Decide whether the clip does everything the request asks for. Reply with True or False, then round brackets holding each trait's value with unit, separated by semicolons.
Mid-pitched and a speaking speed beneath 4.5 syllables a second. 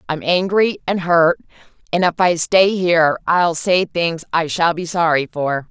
True (170 Hz; 4.2 syllables/s)